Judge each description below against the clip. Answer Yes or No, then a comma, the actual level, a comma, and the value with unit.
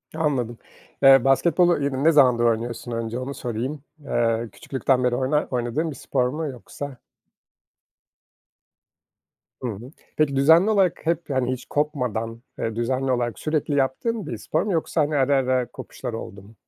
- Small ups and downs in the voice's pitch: No, average, 3.8 semitones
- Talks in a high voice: No, low, 130 Hz